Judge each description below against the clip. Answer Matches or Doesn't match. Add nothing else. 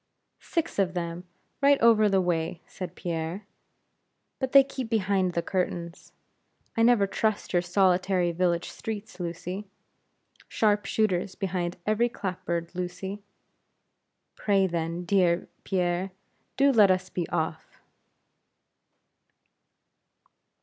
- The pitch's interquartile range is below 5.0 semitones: Matches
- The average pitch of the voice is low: Doesn't match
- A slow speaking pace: Matches